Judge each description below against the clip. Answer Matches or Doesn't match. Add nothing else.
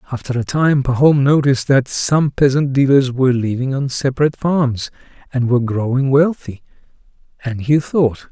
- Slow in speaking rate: Doesn't match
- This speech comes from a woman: Doesn't match